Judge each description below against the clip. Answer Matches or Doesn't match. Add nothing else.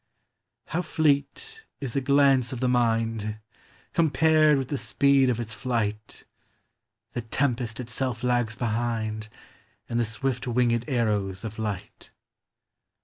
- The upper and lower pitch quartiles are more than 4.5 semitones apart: Doesn't match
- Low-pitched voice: Matches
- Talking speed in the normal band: Doesn't match